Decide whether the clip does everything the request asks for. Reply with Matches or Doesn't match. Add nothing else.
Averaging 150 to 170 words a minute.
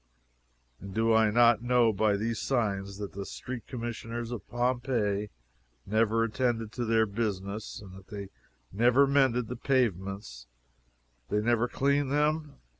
Doesn't match